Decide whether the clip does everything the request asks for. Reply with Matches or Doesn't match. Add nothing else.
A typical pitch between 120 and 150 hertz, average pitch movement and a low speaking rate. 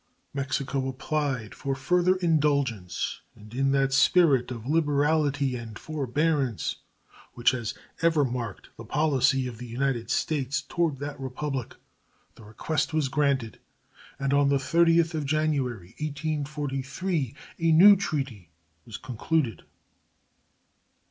Matches